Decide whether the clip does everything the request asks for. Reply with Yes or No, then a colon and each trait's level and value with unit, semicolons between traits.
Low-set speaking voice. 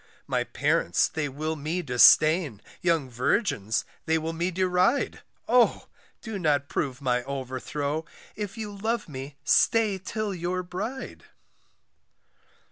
No: medium, 160 Hz